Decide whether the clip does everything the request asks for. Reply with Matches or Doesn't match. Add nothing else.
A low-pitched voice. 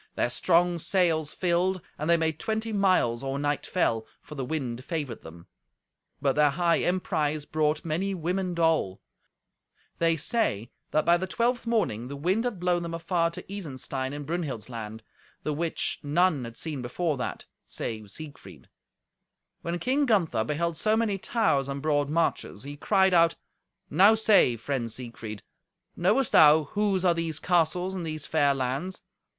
Doesn't match